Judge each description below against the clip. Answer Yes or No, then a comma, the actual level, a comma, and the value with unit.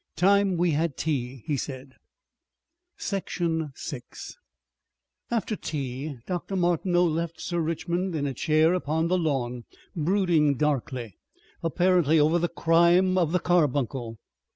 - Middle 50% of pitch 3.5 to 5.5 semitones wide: Yes, average, 3.8 semitones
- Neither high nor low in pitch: Yes, medium, 160 Hz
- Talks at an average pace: No, slow, 125 wpm